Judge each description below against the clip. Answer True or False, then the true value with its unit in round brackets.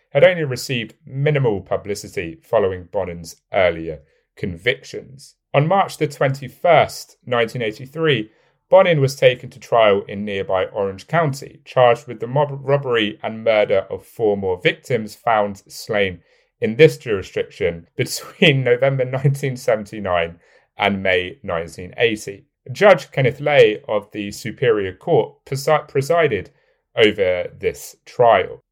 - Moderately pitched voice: False (130 Hz)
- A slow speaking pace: True (120 wpm)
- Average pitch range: False (7.5 semitones)